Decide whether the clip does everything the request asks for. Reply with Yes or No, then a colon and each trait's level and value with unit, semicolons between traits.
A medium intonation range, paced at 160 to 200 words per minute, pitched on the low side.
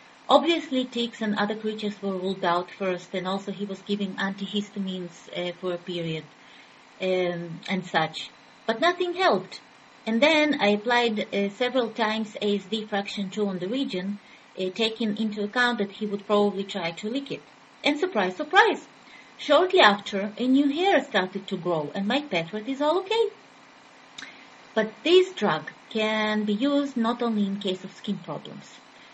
No: average, 4.5 semitones; average, 165 wpm; high, 205 Hz